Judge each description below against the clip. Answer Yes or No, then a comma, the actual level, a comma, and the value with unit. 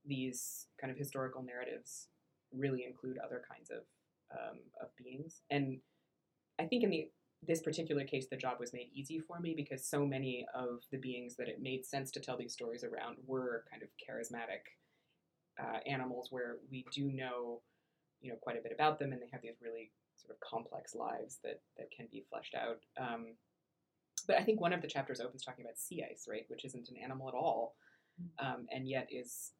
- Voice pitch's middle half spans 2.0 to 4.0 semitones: Yes, narrow, 2.5 semitones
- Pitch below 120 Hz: No, low, 130 Hz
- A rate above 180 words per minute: Yes, average, 200 wpm